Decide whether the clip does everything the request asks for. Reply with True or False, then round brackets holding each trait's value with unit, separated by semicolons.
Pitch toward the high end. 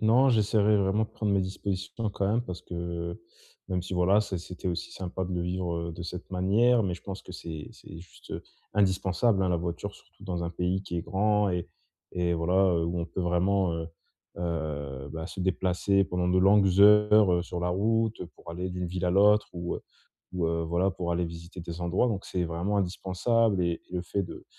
False (90 Hz)